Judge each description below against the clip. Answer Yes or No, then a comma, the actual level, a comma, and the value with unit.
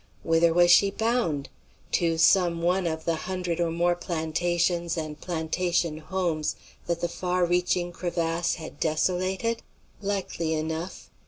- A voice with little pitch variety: Yes, narrow, 1.7 semitones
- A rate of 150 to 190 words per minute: No, slow, 135 wpm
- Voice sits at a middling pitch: Yes, medium, 170 Hz